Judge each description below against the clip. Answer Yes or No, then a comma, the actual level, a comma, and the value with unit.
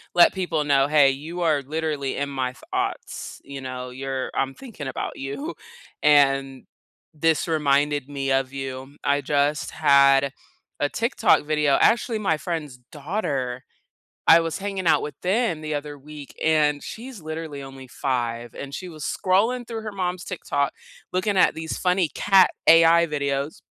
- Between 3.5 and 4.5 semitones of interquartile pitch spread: Yes, average, 3.9 semitones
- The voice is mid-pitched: Yes, medium, 150 Hz